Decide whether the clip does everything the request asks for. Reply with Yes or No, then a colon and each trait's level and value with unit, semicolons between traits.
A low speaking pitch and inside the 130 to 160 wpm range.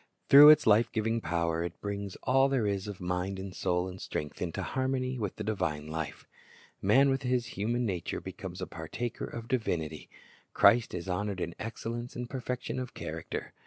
No: low, 105 Hz; average, 180 wpm